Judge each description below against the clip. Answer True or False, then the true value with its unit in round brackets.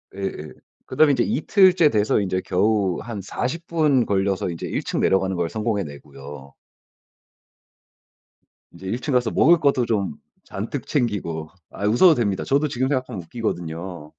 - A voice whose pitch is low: True (105 Hz)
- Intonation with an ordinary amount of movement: False (6.0 semitones)